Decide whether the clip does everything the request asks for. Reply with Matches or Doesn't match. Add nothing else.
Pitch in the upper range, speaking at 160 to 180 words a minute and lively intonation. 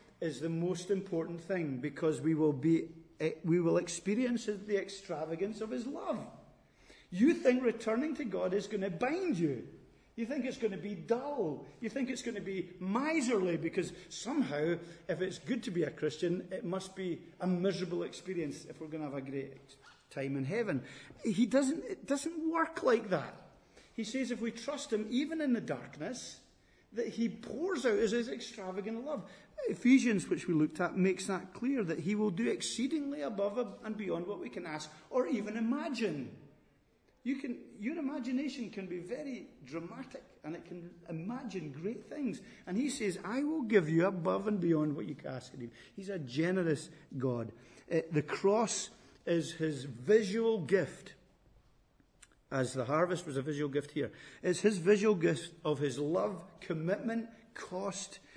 Matches